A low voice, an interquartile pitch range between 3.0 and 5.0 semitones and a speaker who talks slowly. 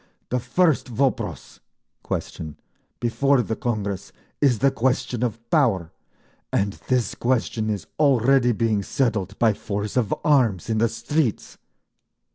Yes: low, 120 Hz; average, 3.7 semitones; slow, 125 wpm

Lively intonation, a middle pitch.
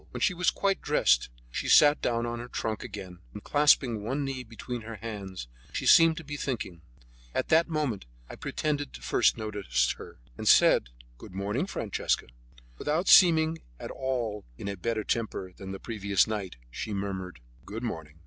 No: wide, 6.7 semitones; low, 115 Hz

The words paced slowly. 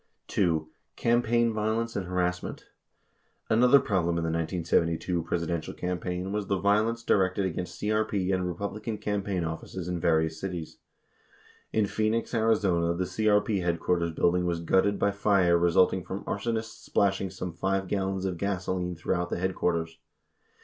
No: average, 145 wpm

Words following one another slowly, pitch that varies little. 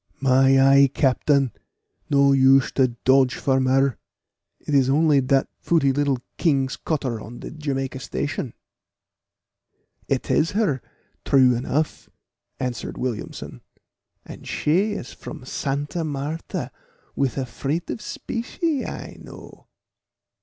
Yes: slow, 120 wpm; narrow, 2.1 semitones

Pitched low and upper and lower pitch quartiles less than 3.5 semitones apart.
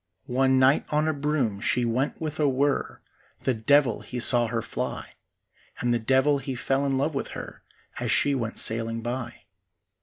Yes: low, 130 Hz; average, 3.0 semitones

